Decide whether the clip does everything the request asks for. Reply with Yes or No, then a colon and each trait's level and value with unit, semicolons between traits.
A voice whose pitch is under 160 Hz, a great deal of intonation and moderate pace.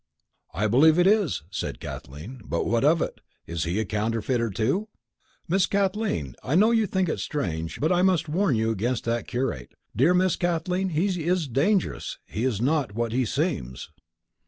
Yes: low, 135 Hz; wide, 8.6 semitones; average, 180 wpm